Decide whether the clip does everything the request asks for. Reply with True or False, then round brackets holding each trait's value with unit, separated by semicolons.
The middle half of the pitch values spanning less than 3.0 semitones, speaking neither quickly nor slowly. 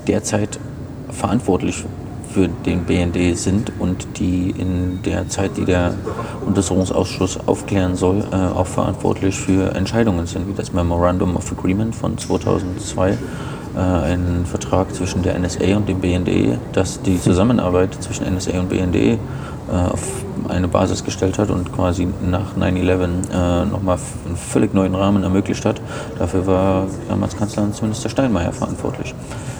True (2.6 semitones; 145 wpm)